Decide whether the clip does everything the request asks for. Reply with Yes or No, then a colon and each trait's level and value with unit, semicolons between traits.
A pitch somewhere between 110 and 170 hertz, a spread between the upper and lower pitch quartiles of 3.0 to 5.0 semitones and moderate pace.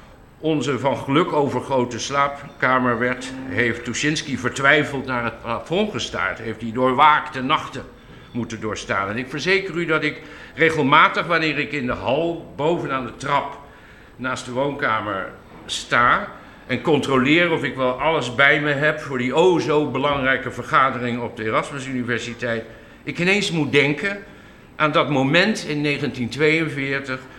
Yes: low, 135 Hz; average, 3.6 semitones; average, 150 wpm